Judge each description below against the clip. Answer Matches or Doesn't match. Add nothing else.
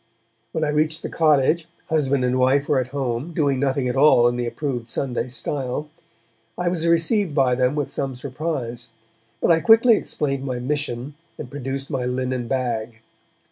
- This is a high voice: Doesn't match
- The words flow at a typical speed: Matches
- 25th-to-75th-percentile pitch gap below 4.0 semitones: Matches